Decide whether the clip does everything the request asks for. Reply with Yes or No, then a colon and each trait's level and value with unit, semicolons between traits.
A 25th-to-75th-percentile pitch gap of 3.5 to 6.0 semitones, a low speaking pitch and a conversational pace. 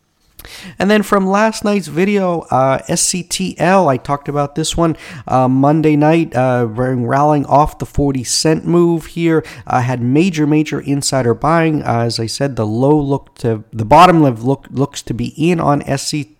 No: average, 4.5 semitones; medium, 145 Hz; average, 170 wpm